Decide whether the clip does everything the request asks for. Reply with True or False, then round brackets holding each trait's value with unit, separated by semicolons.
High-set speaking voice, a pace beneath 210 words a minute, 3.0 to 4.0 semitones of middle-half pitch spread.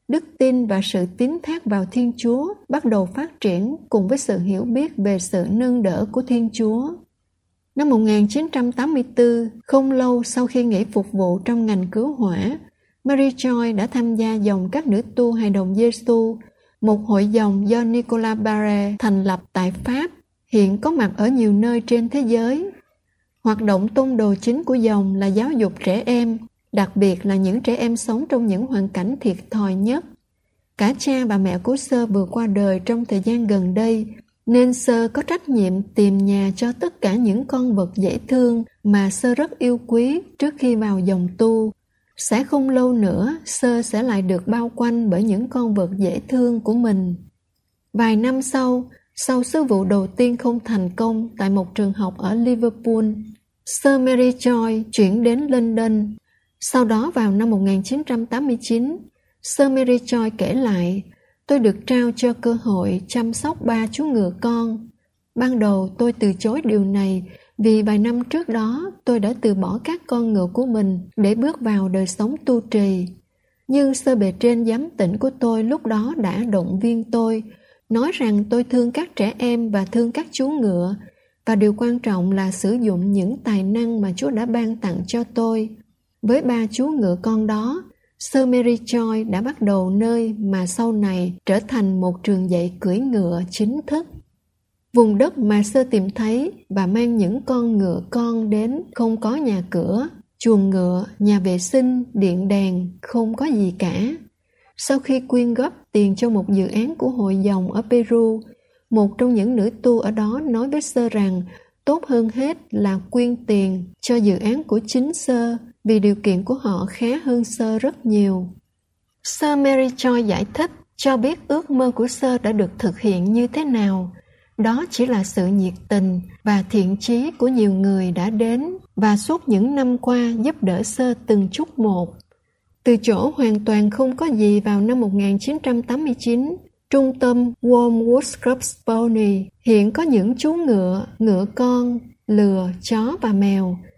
True (225 Hz; 185 wpm; 3.6 semitones)